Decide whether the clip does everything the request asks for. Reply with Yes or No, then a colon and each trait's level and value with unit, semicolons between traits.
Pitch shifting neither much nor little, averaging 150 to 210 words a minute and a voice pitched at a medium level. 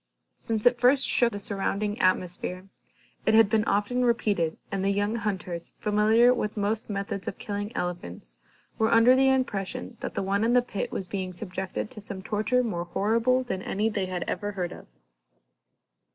No: average, 3.2 semitones; average, 180 wpm; high, 205 Hz